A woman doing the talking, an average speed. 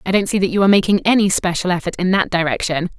No: female; fast, 260 wpm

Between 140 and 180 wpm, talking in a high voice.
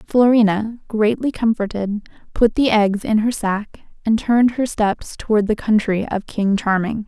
Yes: average, 160 wpm; high, 215 Hz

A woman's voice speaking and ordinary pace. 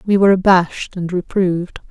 Yes: female; average, 155 wpm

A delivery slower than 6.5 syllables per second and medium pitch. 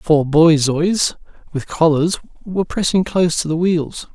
Yes: 4.4 syllables/s; medium, 165 Hz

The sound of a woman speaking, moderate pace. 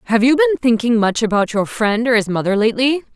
No: female; fast, 230 wpm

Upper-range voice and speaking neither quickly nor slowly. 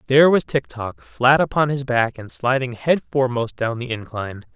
No: low, 125 Hz; average, 185 wpm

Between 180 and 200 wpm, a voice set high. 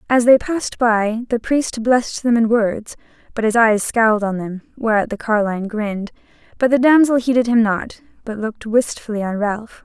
Yes: average, 190 wpm; high, 225 Hz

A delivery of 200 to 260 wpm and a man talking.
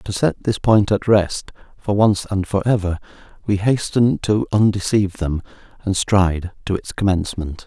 No: average, 165 wpm; male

